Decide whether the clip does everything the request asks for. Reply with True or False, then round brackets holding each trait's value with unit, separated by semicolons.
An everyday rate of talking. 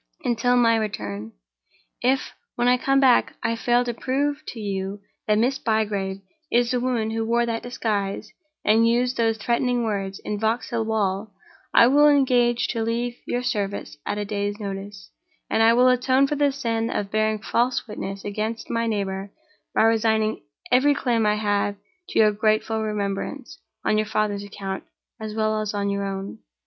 True (175 wpm)